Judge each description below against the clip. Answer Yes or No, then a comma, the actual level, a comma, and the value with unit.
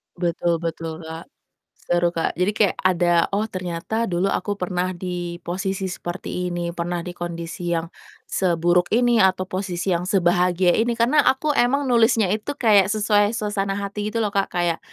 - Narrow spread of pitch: No, average, 3.2 semitones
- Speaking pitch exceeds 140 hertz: Yes, medium, 185 Hz